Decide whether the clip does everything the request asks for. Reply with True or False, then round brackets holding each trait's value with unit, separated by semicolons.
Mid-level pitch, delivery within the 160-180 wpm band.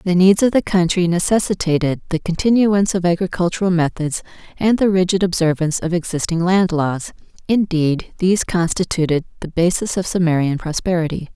False (175 Hz; 145 wpm)